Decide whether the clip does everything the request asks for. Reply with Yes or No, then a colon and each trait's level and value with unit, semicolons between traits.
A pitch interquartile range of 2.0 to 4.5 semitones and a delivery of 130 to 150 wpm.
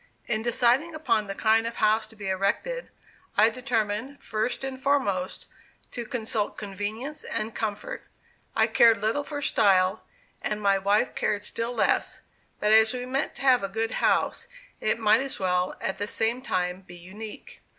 No: average, 3.3 semitones; average, 170 wpm